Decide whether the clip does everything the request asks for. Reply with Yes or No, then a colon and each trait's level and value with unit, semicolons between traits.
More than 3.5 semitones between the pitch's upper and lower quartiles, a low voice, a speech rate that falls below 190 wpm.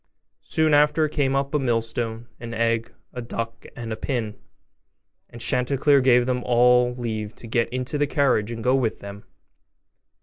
No: average, 2.8 semitones; low, 120 Hz; average, 165 wpm